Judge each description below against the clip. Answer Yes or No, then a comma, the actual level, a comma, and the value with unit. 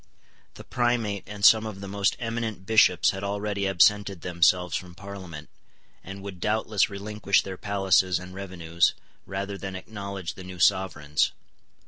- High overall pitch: No, low, 100 Hz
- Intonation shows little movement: Yes, narrow, 1.9 semitones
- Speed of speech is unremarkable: Yes, average, 145 wpm